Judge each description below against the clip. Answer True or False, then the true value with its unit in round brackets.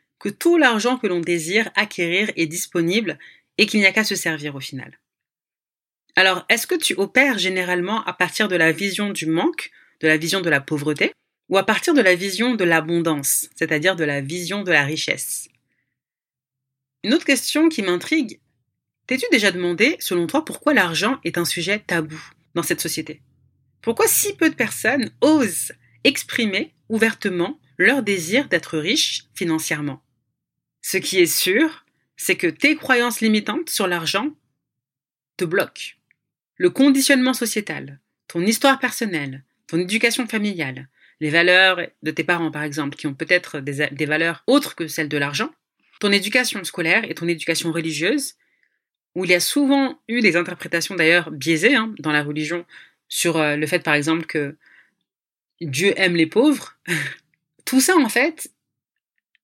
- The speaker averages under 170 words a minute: True (160 wpm)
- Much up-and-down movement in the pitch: True (7.0 semitones)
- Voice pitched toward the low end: False (180 Hz)